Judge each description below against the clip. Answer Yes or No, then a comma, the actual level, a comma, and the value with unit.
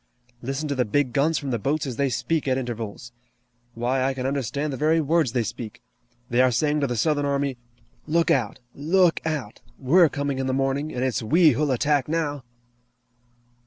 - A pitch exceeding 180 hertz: No, medium, 140 Hz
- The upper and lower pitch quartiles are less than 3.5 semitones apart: Yes, average, 3.1 semitones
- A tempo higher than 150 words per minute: Yes, average, 195 wpm